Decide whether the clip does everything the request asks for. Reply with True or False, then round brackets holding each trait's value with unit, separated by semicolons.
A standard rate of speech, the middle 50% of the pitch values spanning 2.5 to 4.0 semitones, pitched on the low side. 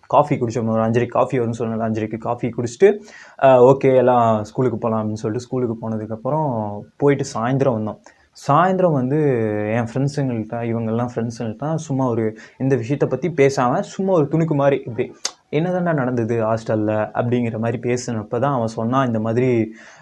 False (145 wpm; 3.4 semitones; 120 Hz)